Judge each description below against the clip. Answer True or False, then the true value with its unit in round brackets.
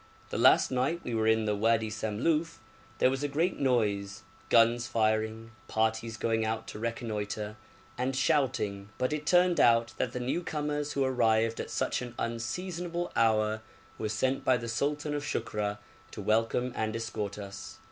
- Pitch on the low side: True (115 Hz)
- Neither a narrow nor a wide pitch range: True (3.5 semitones)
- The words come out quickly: False (165 wpm)